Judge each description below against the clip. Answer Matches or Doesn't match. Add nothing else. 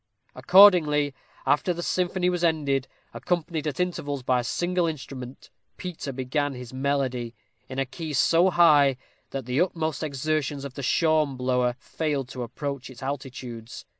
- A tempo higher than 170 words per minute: Doesn't match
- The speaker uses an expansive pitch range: Doesn't match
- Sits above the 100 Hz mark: Matches